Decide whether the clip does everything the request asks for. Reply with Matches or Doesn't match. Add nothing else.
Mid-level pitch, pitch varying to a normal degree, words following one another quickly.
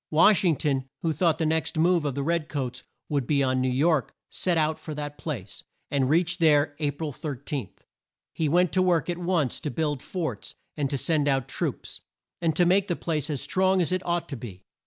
Matches